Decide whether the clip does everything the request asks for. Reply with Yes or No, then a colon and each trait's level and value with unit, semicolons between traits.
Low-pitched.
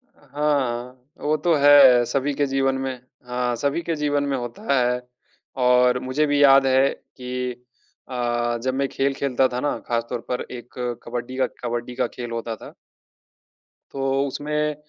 Yes: low, 130 Hz